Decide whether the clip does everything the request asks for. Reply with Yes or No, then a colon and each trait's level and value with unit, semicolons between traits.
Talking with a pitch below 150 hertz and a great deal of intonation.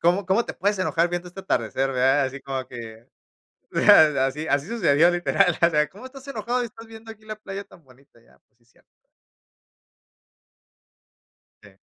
No: medium, 175 Hz; wide, 7.8 semitones